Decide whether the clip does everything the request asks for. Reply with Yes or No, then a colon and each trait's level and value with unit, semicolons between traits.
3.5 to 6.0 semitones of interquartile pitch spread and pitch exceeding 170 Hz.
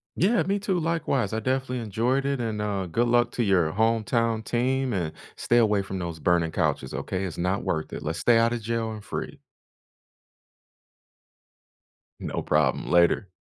No: average, 4.5 semitones; low, 110 Hz